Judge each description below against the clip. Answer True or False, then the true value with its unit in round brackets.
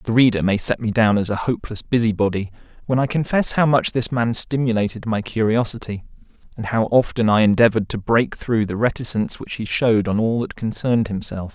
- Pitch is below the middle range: True (115 Hz)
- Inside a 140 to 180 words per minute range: False (195 wpm)